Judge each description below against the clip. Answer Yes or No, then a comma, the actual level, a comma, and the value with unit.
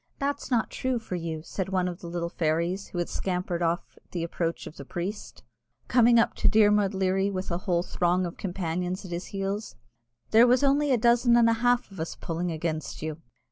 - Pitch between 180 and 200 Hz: Yes, medium, 185 Hz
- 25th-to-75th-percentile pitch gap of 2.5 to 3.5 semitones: No, average, 4.6 semitones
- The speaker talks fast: Yes, fast, 215 wpm